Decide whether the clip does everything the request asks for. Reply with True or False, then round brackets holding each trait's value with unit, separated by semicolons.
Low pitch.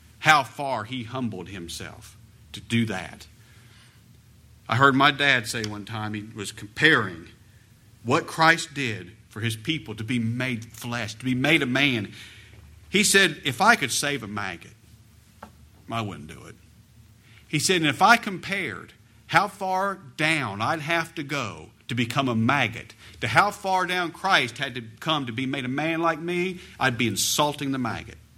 True (120 Hz)